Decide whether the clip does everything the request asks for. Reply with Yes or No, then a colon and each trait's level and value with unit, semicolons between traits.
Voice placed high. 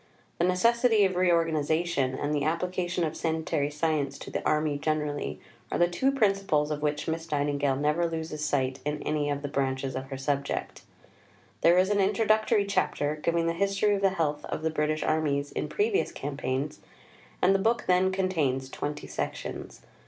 No: medium, 155 Hz